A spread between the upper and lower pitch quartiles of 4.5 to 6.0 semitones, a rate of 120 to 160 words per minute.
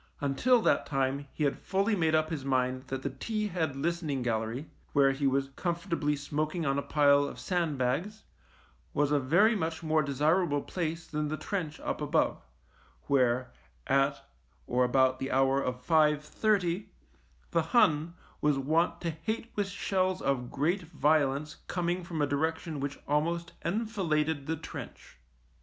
No: average, 3.8 semitones; average, 155 wpm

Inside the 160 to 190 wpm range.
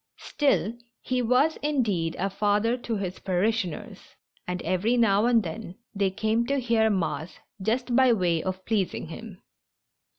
No: average, 145 wpm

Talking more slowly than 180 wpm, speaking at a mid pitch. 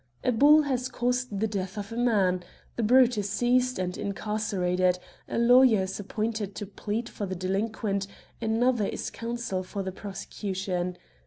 No: average, 165 wpm; high, 210 Hz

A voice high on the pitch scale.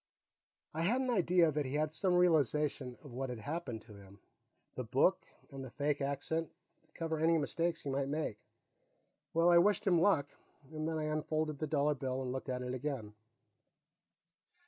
No: medium, 150 Hz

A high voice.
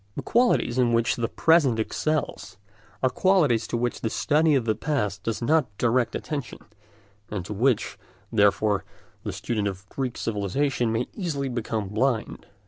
No: low, 120 Hz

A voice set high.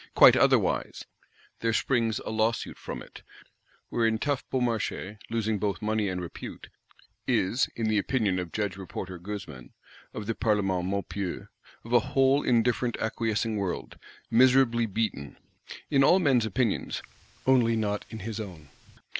No: low, 110 Hz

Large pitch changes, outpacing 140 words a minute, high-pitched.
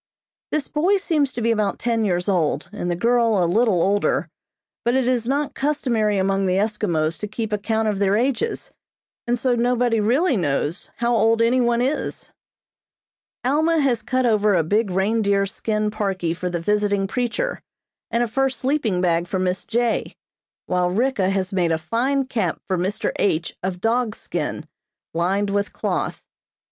No: average, 4.3 semitones; average, 170 wpm; high, 215 Hz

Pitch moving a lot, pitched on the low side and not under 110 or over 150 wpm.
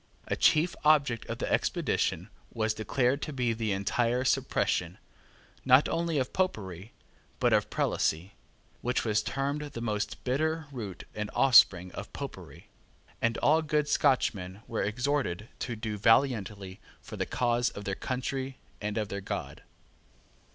No: average, 4.8 semitones; low, 115 Hz; average, 145 wpm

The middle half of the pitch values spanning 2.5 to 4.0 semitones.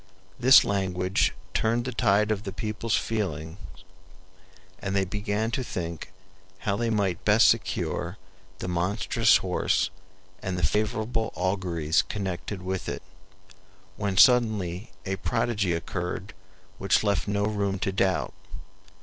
Yes: average, 2.9 semitones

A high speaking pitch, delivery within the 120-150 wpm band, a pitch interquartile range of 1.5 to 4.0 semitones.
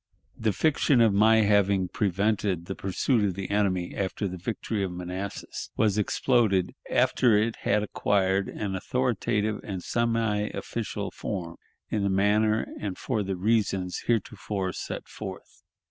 No: low, 100 Hz; average, 145 wpm; narrow, 2.5 semitones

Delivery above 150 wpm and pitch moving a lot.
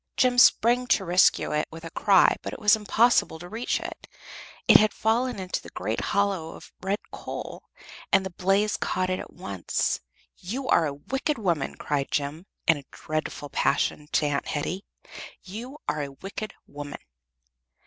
Yes: average, 170 wpm; wide, 6.0 semitones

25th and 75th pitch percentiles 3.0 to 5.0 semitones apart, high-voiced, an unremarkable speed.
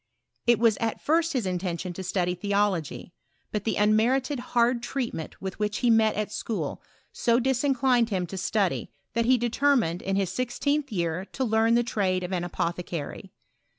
Yes: average, 4.7 semitones; high, 215 Hz; average, 155 wpm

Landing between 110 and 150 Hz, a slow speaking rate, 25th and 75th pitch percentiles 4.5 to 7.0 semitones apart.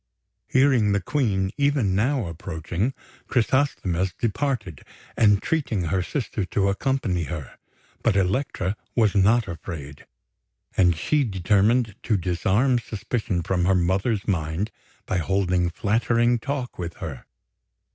No: low, 100 Hz; slow, 115 wpm; average, 5.1 semitones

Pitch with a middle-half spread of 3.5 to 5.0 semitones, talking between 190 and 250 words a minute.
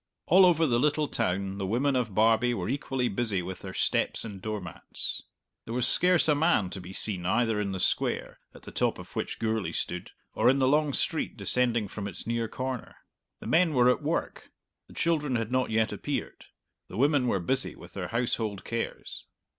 Yes: average, 4.7 semitones; average, 200 wpm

